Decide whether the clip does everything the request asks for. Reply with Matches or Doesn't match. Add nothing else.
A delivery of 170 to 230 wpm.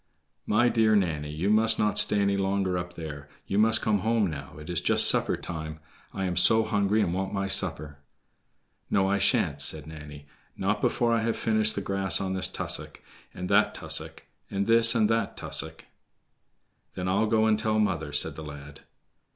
Matches